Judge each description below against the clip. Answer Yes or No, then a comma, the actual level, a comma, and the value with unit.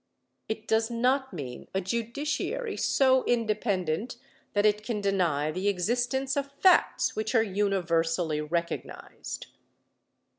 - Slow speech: Yes, slow, 115 wpm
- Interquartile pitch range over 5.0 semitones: Yes, wide, 5.4 semitones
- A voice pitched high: Yes, high, 215 Hz